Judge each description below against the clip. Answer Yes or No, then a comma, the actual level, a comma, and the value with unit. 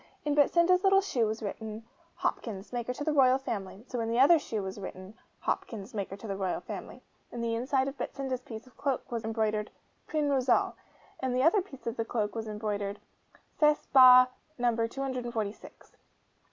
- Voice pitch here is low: No, high, 240 Hz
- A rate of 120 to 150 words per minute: No, average, 180 wpm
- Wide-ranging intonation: No, average, 3.8 semitones